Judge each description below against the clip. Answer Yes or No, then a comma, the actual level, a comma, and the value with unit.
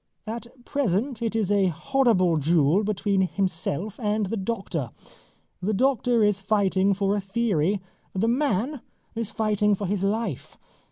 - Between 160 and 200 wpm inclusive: No, average, 145 wpm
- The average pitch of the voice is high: Yes, high, 205 Hz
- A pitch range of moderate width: Yes, average, 3.1 semitones